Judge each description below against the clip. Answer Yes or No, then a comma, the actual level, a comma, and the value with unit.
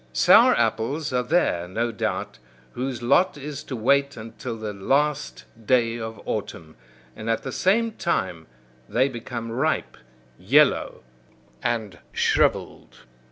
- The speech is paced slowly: Yes, slow, 125 wpm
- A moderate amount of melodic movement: Yes, average, 4.1 semitones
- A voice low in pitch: Yes, low, 120 Hz